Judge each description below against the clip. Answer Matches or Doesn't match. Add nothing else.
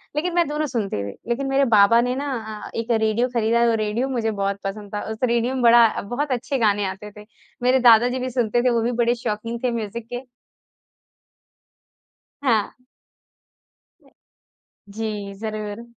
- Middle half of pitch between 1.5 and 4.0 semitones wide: Matches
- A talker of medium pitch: Doesn't match